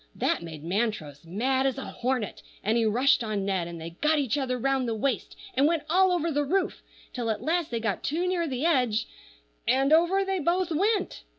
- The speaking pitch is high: Yes, very high, 265 Hz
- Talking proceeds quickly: Yes, fast, 210 wpm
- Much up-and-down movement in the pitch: Yes, wide, 7.2 semitones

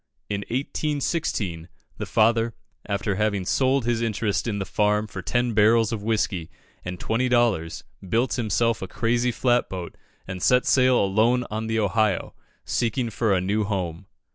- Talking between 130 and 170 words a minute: Yes, average, 160 wpm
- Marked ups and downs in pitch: No, average, 3.4 semitones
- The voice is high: No, low, 110 Hz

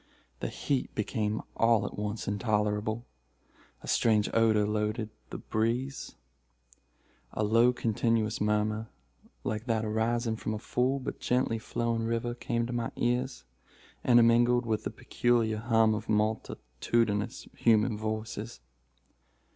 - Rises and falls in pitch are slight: Yes, narrow, 1.7 semitones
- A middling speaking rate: No, slow, 125 wpm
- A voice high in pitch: No, low, 110 Hz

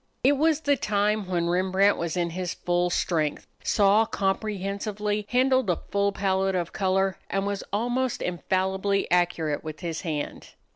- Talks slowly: No, average, 150 wpm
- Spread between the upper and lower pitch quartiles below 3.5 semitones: Yes, average, 2.9 semitones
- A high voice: Yes, high, 195 Hz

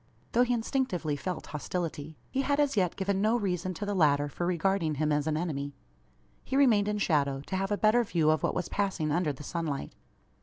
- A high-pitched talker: No, medium, 180 Hz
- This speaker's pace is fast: Yes, fast, 215 wpm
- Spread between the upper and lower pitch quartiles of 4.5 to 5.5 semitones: Yes, average, 5.2 semitones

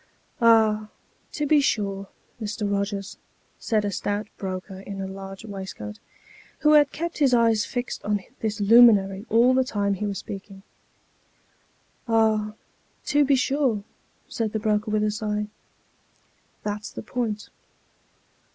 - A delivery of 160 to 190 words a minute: No, average, 150 wpm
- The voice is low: No, high, 210 Hz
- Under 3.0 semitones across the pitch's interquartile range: Yes, narrow, 2.6 semitones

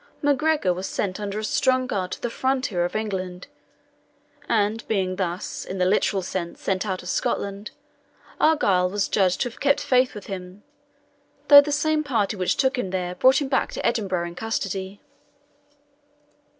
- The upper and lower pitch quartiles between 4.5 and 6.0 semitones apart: Yes, wide, 5.5 semitones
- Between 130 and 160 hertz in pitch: No, high, 200 Hz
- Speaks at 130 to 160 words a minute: No, average, 170 wpm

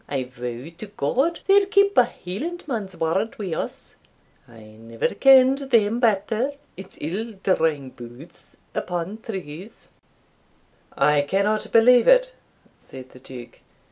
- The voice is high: Yes, high, 195 Hz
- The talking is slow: Yes, slow, 125 wpm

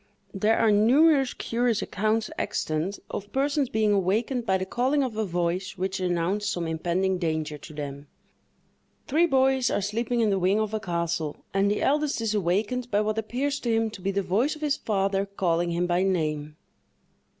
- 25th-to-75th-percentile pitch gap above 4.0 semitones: Yes, average, 4.8 semitones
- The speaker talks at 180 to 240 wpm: Yes, average, 185 wpm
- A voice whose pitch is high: Yes, high, 205 Hz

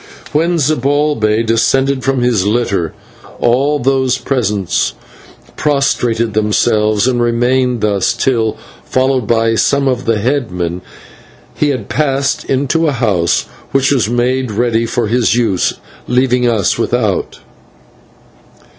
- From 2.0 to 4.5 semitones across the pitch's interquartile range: Yes, average, 3.3 semitones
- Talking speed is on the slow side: Yes, slow, 120 wpm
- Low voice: Yes, low, 120 Hz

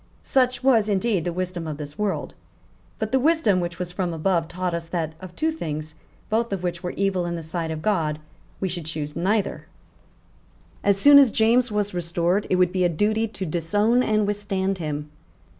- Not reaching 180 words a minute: No, average, 195 wpm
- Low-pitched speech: No, medium, 185 Hz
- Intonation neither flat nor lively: Yes, average, 4.0 semitones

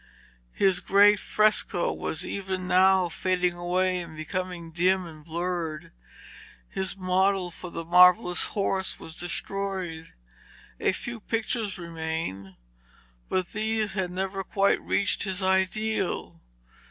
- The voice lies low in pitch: No, medium, 185 Hz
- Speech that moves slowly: Yes, slow, 115 wpm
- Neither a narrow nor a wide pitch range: No, narrow, 2.0 semitones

